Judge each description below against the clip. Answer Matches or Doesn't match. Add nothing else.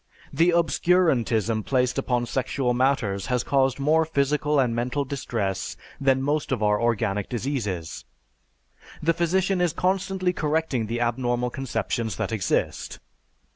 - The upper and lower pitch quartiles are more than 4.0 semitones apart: Matches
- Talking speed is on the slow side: Matches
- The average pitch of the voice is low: Matches